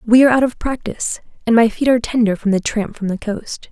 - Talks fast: Yes, fast, 260 wpm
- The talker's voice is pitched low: No, high, 230 Hz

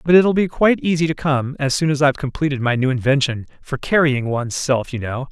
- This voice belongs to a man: Yes, male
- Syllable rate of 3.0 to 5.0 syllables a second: No, 6.0 syllables/s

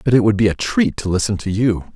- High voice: No, low, 110 Hz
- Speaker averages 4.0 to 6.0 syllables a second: No, 6.3 syllables/s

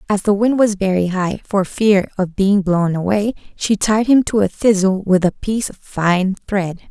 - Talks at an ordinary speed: No, fast, 210 wpm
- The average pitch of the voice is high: Yes, high, 195 Hz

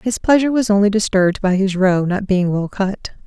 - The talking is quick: Yes, fast, 220 wpm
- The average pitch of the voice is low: No, high, 200 Hz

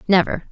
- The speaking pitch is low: No, medium, 185 Hz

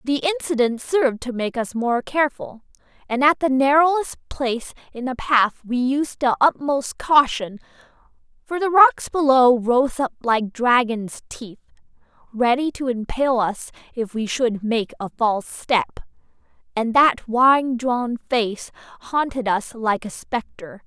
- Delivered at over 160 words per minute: No, average, 145 wpm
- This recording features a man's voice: No, female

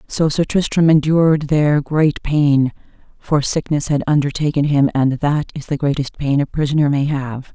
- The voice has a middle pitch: Yes, medium, 145 Hz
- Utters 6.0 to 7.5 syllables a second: No, 4.8 syllables/s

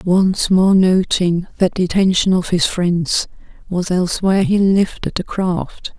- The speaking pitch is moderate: Yes, medium, 180 Hz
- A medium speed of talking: Yes, average, 150 wpm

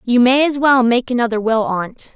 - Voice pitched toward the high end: Yes, high, 240 Hz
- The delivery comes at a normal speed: No, fast, 225 wpm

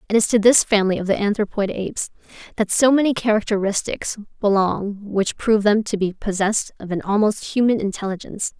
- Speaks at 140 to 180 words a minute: Yes, average, 175 wpm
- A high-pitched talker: Yes, high, 210 Hz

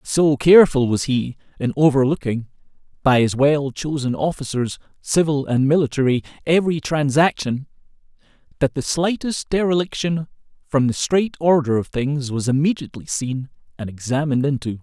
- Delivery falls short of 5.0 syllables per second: No, 5.1 syllables/s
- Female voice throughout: No, male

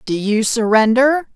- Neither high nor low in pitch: No, high, 235 Hz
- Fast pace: No, slow, 135 wpm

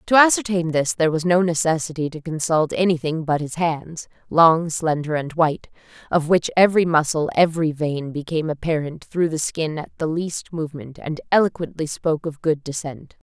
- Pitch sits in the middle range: Yes, medium, 160 Hz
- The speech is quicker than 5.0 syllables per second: Yes, 5.3 syllables/s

